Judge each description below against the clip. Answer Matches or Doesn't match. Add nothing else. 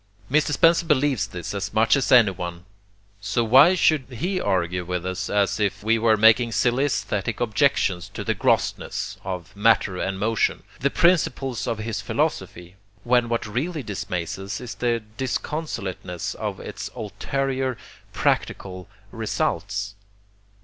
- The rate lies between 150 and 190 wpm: Doesn't match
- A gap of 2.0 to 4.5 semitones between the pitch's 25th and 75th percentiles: Doesn't match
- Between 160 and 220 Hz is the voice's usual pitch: Doesn't match